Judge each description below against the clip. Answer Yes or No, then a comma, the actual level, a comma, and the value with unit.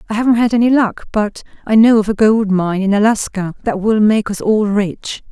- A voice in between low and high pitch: No, high, 210 Hz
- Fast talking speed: Yes, fast, 225 wpm